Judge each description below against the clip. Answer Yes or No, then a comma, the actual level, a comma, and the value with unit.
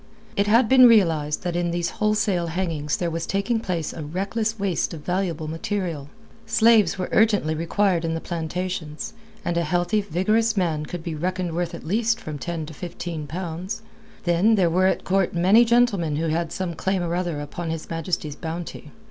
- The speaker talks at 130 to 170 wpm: No, average, 185 wpm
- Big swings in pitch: No, average, 3.4 semitones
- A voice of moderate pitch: Yes, medium, 175 Hz